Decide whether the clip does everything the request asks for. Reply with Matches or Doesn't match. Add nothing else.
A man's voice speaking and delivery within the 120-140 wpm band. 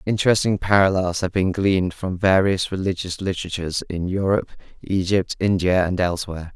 Matches